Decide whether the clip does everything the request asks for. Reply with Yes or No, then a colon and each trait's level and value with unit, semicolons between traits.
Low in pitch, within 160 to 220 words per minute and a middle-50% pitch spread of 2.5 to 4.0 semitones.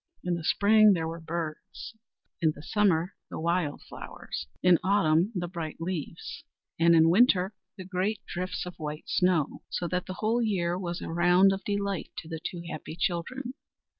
No: medium, 175 Hz; average, 175 wpm; average, 2.8 semitones